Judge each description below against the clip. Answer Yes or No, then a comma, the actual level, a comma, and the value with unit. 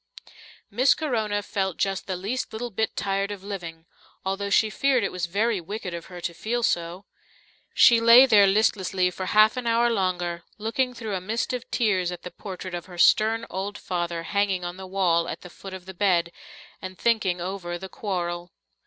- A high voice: Yes, high, 195 Hz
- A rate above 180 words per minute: Yes, average, 195 wpm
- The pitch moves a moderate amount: Yes, average, 3.5 semitones